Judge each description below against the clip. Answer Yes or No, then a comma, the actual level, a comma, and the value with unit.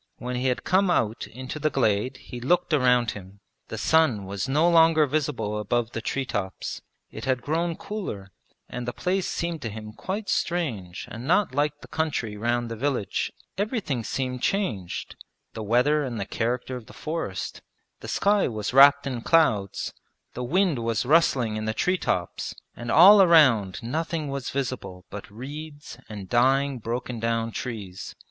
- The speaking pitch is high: No, low, 125 Hz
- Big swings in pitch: Yes, wide, 5.7 semitones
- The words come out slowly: No, average, 170 wpm